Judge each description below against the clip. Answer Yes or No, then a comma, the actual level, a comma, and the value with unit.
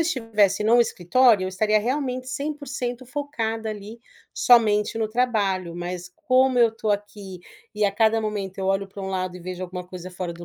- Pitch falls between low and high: No, high, 215 Hz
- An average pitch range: Yes, average, 4.3 semitones